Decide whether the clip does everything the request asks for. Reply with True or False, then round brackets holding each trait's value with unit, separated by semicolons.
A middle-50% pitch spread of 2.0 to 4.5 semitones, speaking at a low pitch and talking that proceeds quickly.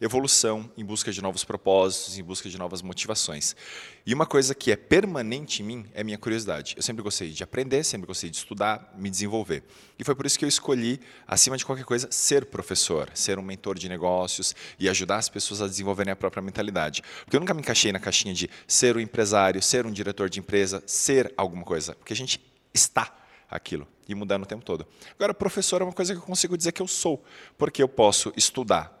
False (5.4 semitones; 105 Hz; 220 wpm)